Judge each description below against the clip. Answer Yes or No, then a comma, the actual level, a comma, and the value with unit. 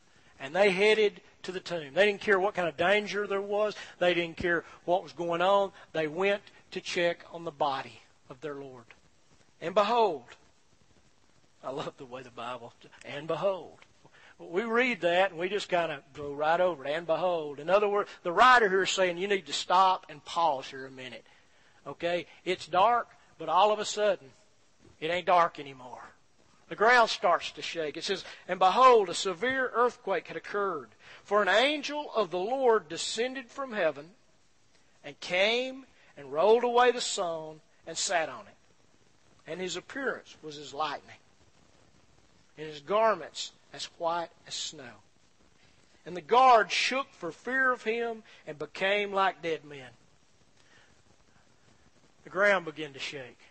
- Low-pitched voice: No, medium, 180 Hz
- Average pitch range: Yes, average, 5.0 semitones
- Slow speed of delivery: No, average, 170 wpm